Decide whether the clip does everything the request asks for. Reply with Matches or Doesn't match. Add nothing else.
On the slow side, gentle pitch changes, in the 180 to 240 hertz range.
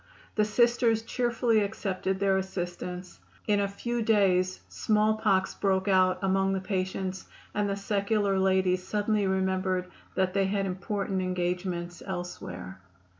Matches